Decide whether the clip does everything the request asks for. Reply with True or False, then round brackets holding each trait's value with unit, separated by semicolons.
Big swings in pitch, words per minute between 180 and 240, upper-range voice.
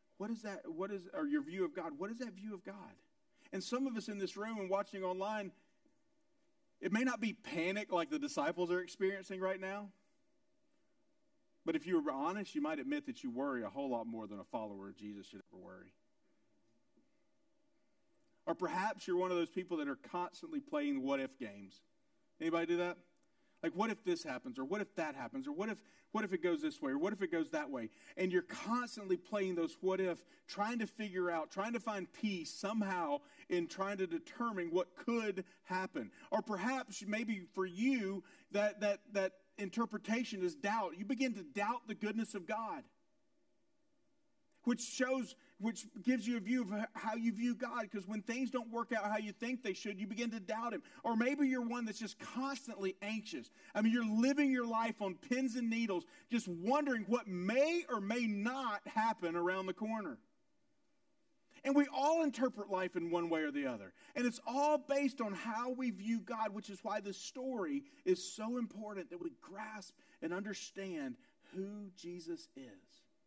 True (7.0 semitones; 195 wpm; 230 Hz)